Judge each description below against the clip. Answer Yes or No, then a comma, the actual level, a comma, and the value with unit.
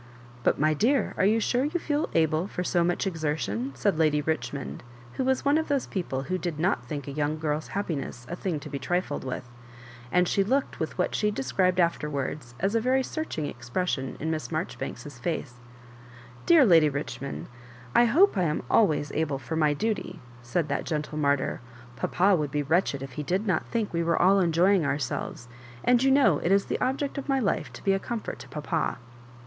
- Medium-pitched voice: Yes, medium, 160 Hz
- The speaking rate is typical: No, fast, 210 wpm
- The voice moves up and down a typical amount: No, wide, 5.9 semitones